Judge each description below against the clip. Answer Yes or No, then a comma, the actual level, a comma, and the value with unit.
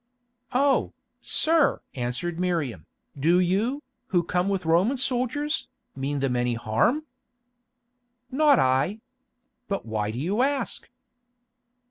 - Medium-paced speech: No, slow, 110 wpm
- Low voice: No, medium, 180 Hz